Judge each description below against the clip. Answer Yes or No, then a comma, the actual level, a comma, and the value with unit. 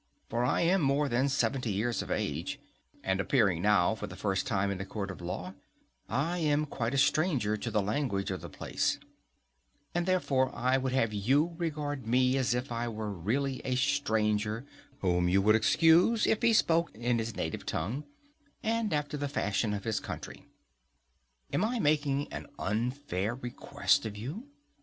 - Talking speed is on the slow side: No, average, 175 wpm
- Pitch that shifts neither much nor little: No, wide, 5.8 semitones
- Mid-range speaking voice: No, low, 120 Hz